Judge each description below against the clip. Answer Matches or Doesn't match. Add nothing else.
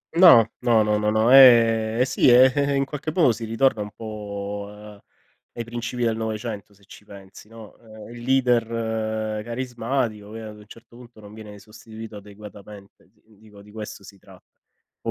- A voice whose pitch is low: Matches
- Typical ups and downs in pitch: Doesn't match